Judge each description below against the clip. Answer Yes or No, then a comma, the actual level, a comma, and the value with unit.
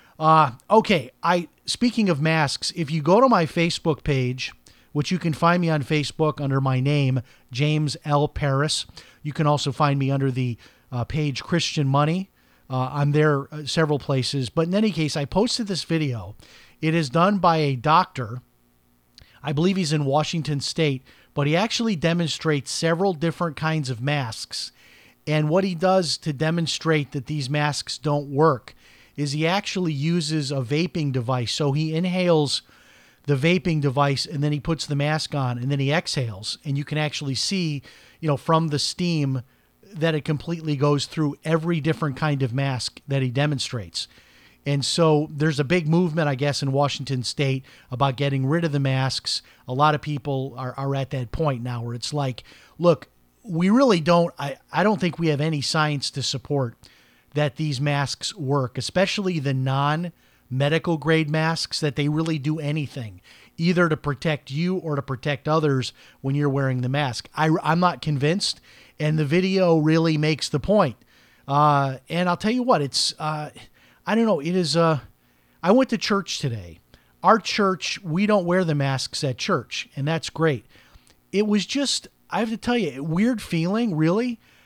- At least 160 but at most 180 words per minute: Yes, average, 175 wpm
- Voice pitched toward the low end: No, medium, 150 Hz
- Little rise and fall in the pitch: No, average, 3.5 semitones